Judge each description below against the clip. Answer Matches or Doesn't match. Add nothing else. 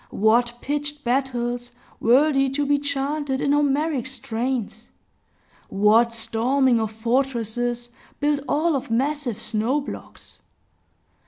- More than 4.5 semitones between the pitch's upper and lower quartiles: Doesn't match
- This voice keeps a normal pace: Doesn't match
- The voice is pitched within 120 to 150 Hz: Doesn't match